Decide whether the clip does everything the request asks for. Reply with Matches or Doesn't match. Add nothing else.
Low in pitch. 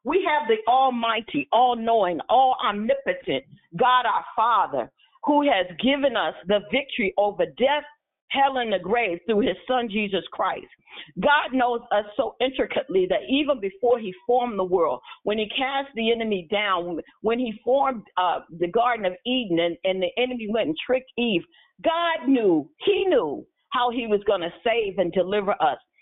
Doesn't match